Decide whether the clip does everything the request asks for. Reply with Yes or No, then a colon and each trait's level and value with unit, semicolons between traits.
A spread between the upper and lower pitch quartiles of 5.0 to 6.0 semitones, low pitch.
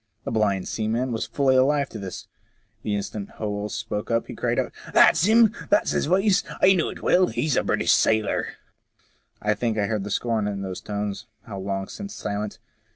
Yes: wide, 5.4 semitones; low, 110 Hz